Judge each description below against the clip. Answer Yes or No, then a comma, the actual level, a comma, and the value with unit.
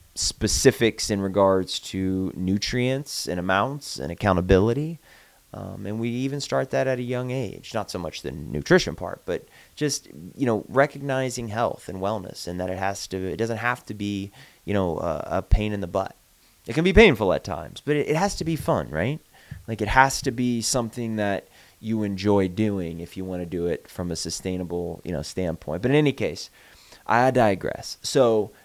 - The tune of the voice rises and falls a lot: Yes, wide, 5.8 semitones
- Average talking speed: Yes, average, 195 wpm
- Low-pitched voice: Yes, low, 105 Hz